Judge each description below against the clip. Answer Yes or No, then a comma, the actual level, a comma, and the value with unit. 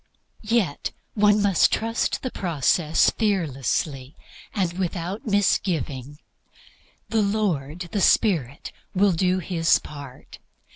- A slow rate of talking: Yes, slow, 100 wpm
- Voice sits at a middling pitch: Yes, medium, 180 Hz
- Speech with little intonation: No, wide, 5.6 semitones